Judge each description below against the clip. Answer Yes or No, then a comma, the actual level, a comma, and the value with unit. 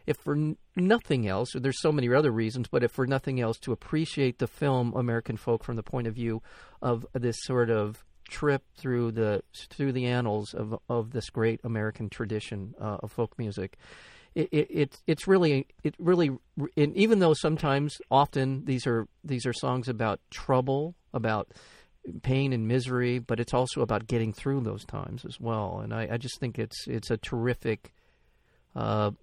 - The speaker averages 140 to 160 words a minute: No, average, 185 wpm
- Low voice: Yes, low, 125 Hz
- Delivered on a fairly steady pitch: No, average, 3.5 semitones